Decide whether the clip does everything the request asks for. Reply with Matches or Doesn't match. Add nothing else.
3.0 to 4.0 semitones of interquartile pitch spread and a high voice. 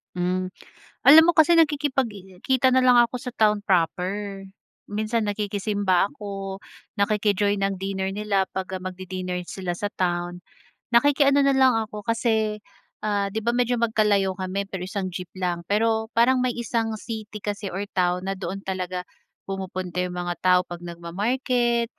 Matches